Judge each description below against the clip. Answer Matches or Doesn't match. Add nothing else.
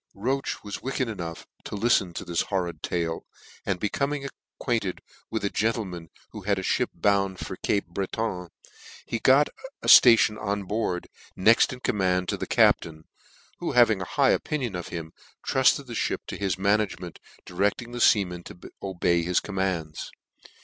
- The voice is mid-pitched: Doesn't match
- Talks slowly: Doesn't match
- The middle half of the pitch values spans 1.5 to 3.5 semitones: Doesn't match